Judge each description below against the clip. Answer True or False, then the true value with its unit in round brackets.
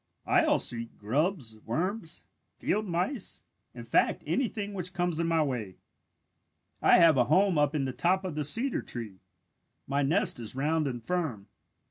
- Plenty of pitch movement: True (6.1 semitones)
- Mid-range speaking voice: True (160 Hz)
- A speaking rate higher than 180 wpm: False (165 wpm)